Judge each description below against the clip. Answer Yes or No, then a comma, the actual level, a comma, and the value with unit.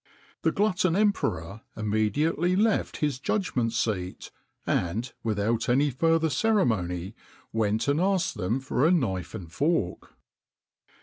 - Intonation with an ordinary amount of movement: No, wide, 8.0 semitones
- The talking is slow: Yes, slow, 120 wpm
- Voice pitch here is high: No, low, 125 Hz